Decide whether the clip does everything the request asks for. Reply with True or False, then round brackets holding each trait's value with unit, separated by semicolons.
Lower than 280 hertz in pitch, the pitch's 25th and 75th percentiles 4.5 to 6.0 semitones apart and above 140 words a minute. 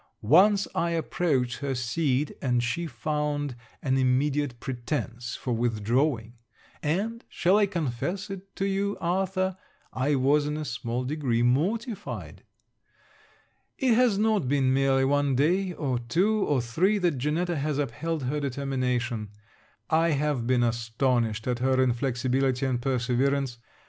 False (140 Hz; 5.2 semitones; 135 wpm)